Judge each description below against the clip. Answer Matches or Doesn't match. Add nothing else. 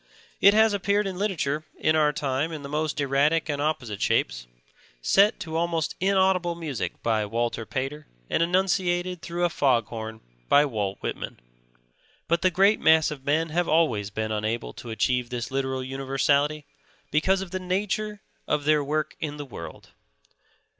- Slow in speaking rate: Doesn't match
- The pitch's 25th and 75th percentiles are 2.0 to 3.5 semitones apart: Doesn't match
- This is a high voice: Doesn't match